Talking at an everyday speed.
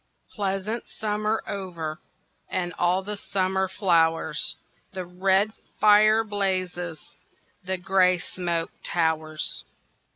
No: slow, 95 wpm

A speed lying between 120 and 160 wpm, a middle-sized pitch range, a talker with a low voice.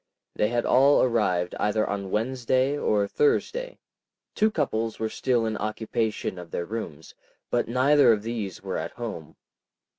Yes: average, 150 wpm; average, 3.9 semitones; low, 115 Hz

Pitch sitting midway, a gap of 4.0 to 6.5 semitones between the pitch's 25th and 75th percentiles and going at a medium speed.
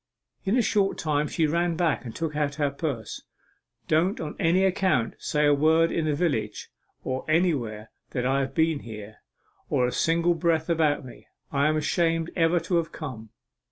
No: medium, 155 Hz; average, 3.5 semitones; average, 180 wpm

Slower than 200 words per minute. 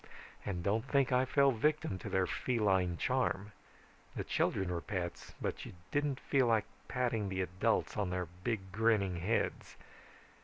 Yes: average, 155 wpm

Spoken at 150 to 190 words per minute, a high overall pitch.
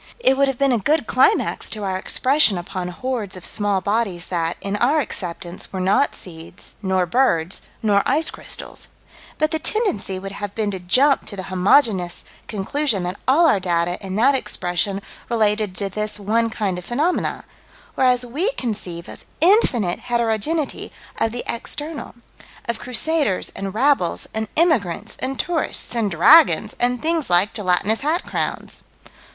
Yes: average, 160 wpm; high, 215 Hz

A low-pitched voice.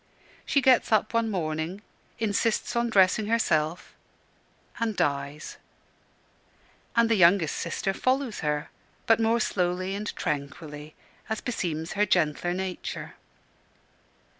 No: high, 190 Hz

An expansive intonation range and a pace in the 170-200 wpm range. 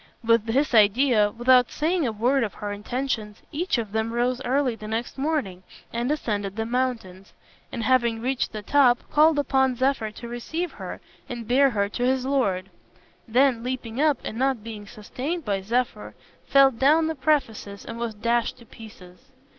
No: average, 3.6 semitones; average, 175 wpm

